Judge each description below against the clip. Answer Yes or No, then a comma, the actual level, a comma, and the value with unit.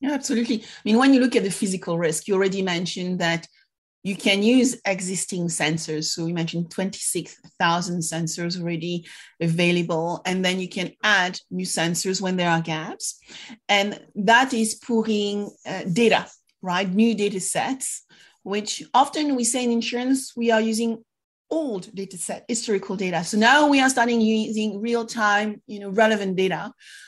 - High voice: Yes, high, 200 Hz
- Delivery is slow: No, average, 165 wpm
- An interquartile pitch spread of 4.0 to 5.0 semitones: Yes, average, 4.5 semitones